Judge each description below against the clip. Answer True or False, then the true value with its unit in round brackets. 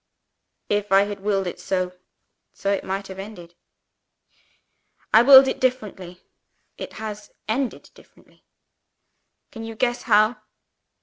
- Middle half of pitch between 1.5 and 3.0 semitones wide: True (2.6 semitones)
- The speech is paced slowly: True (125 wpm)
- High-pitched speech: True (210 Hz)